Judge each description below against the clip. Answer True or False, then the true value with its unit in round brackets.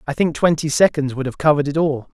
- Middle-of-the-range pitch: True (150 Hz)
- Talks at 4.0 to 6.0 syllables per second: False (6.5 syllables/s)